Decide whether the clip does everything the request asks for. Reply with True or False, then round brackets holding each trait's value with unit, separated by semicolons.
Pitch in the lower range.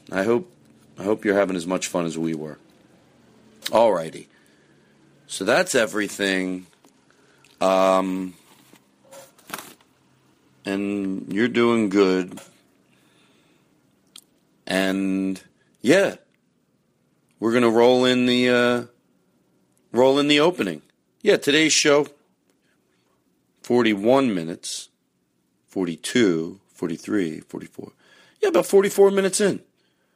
True (100 Hz)